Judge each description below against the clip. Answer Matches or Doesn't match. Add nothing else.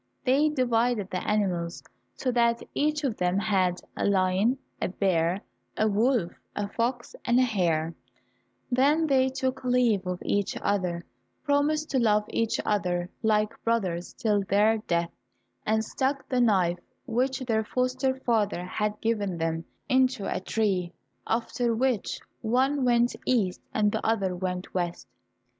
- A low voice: Doesn't match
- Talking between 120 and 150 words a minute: Matches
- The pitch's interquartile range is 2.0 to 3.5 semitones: Doesn't match